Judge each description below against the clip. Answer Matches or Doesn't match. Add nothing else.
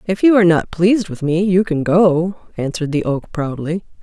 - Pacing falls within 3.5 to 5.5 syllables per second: Matches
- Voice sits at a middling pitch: Matches